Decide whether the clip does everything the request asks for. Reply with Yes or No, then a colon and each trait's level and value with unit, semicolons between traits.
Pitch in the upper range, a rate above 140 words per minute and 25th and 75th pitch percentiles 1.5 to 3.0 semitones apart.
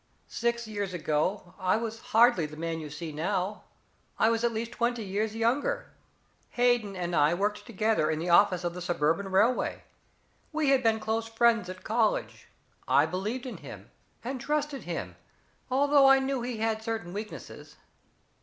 No: high, 220 Hz; average, 165 wpm; average, 4.7 semitones